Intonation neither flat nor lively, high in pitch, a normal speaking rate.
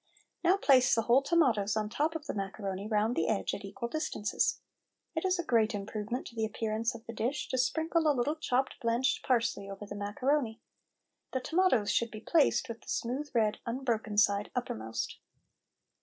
Yes: average, 4.5 semitones; high, 235 Hz; average, 185 wpm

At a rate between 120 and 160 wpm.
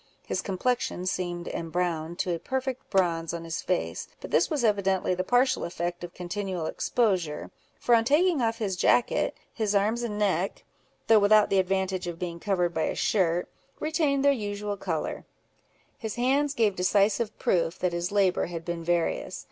No: average, 170 wpm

